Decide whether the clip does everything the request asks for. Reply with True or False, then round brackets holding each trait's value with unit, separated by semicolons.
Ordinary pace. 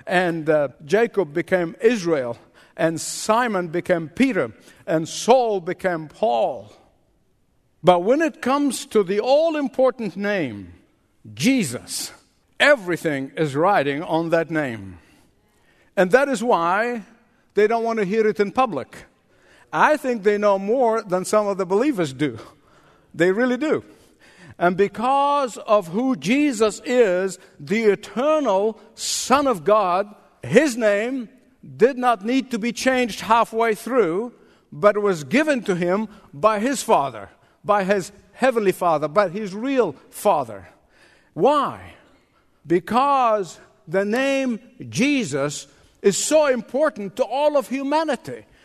False (130 wpm)